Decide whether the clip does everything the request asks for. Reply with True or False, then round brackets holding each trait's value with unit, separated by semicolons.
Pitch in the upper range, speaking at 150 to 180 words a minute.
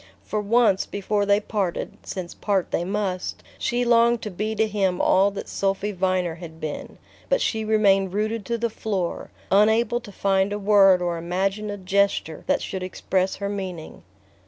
True (200 Hz; 175 wpm)